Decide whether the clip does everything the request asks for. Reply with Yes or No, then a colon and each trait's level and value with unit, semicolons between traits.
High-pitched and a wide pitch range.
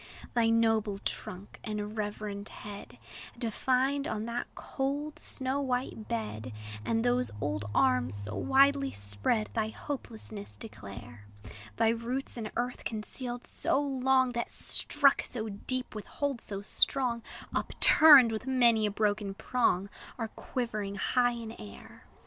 No: high, 225 Hz; average, 3.9 semitones